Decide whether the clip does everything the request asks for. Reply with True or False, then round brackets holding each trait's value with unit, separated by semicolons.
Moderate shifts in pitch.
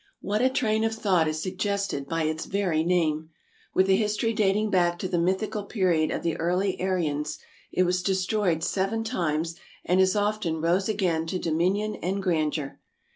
True (3.7 semitones)